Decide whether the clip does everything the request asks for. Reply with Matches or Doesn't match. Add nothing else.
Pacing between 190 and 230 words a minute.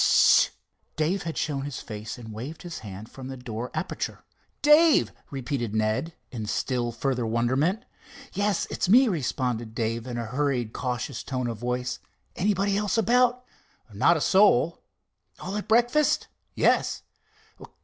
Doesn't match